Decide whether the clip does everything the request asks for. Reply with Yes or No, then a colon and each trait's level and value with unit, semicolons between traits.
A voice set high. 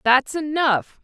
Yes: very high, 275 Hz